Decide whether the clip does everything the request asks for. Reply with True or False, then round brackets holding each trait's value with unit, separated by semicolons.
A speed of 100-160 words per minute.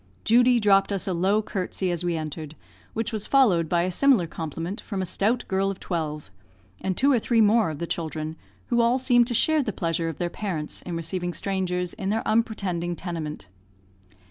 False (195 wpm)